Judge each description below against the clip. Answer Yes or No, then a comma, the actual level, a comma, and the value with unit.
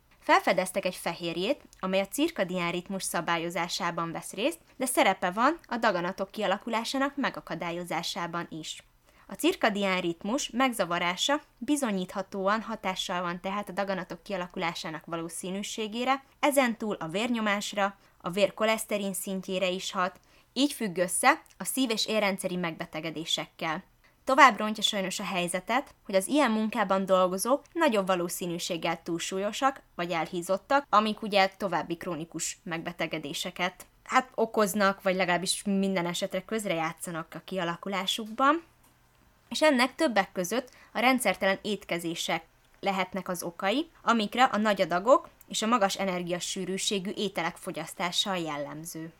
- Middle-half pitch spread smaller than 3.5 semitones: No, average, 3.9 semitones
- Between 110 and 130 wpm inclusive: Yes, average, 120 wpm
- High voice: Yes, high, 195 Hz